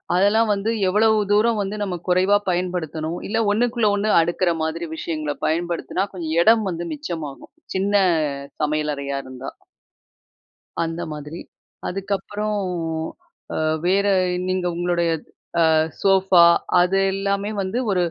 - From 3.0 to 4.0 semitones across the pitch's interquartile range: Yes, average, 3.5 semitones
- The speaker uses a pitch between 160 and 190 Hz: Yes, medium, 185 Hz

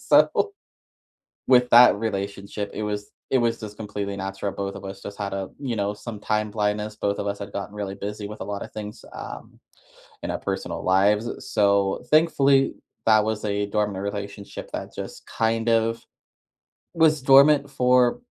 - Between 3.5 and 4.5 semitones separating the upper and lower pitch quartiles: No, narrow, 2.4 semitones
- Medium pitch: No, low, 105 Hz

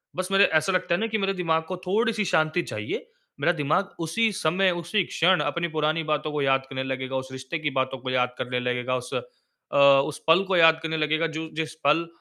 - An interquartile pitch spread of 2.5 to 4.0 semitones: No, average, 5.3 semitones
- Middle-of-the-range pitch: Yes, medium, 160 Hz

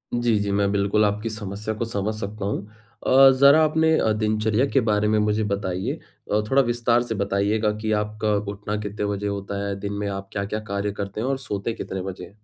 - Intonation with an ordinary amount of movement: No, narrow, 1.8 semitones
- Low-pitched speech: Yes, low, 105 Hz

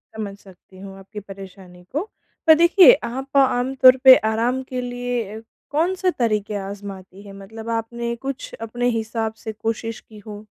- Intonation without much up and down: No, average, 4.0 semitones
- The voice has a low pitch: No, high, 225 Hz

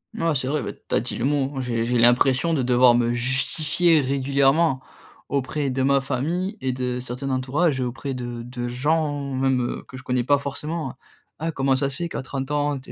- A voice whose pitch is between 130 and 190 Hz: Yes, low, 135 Hz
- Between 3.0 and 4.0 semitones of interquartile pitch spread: No, narrow, 2.4 semitones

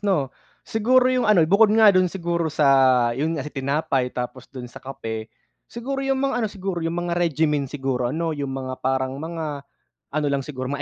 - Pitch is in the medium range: Yes, medium, 150 Hz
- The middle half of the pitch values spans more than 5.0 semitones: Yes, wide, 5.6 semitones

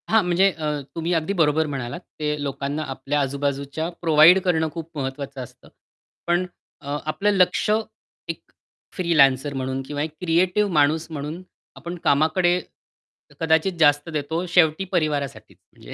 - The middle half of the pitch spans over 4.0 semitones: No, average, 3.4 semitones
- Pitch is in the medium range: Yes, medium, 155 Hz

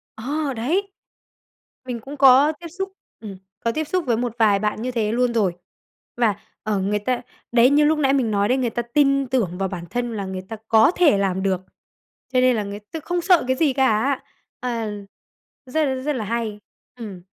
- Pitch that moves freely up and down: No, average, 4.6 semitones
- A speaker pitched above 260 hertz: No, high, 240 Hz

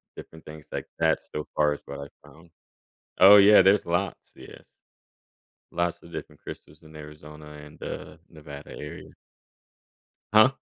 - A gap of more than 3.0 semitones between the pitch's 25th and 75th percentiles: No, average, 2.7 semitones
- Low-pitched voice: Yes, very low, 80 Hz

